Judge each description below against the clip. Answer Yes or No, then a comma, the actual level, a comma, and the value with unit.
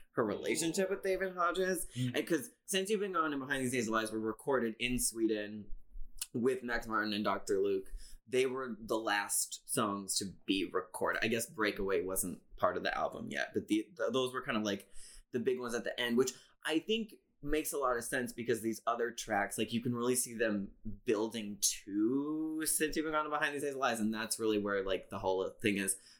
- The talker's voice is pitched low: Yes, low, 125 Hz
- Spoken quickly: Yes, fast, 220 wpm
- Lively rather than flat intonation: Yes, wide, 6.1 semitones